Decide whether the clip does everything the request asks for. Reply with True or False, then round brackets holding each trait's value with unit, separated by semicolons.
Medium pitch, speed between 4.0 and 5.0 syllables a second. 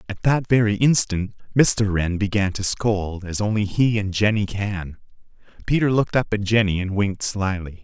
False (105 Hz; 4.9 syllables/s)